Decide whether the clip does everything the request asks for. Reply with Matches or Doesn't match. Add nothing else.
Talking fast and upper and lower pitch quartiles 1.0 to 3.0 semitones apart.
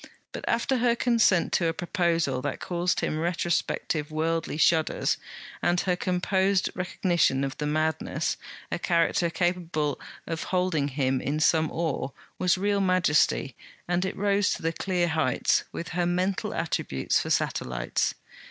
Doesn't match